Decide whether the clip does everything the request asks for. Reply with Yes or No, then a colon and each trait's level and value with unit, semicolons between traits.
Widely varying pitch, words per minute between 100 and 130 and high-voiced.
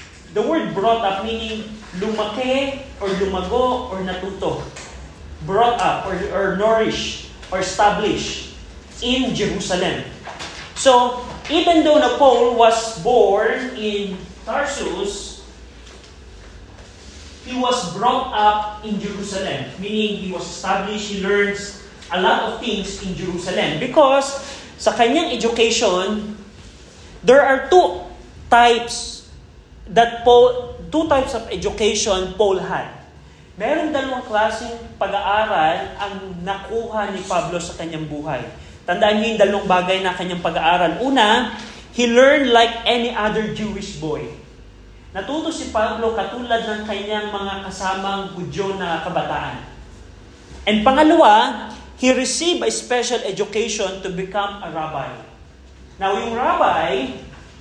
No: average, 4.2 semitones; average, 115 wpm; high, 210 Hz